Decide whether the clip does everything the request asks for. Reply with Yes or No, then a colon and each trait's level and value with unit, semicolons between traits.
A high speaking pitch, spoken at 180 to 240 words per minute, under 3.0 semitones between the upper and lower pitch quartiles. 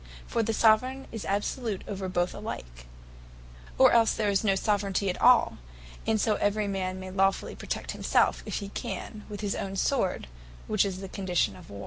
Yes: high, 200 Hz; average, 185 wpm; narrow, 2.4 semitones